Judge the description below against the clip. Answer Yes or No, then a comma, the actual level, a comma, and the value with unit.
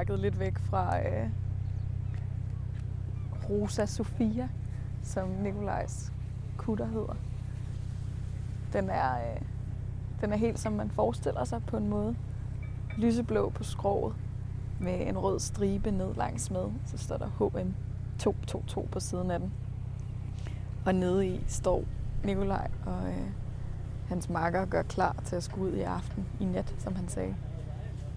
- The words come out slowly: Yes, slow, 135 wpm